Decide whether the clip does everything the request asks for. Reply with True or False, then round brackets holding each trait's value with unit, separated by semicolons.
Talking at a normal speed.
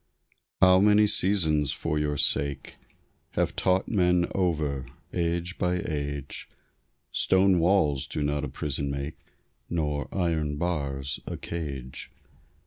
False (120 wpm)